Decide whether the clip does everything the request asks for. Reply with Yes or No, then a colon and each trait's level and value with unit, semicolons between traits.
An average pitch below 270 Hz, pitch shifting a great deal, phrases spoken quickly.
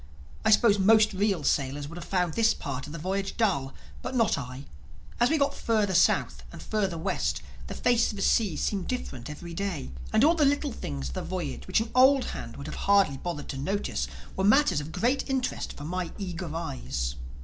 Yes: medium, 185 Hz; wide, 7.8 semitones; fast, 210 wpm